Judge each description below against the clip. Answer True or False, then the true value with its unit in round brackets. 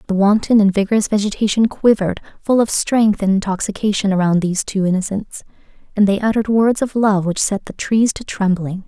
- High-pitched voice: True (205 Hz)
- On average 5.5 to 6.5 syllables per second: True (5.8 syllables/s)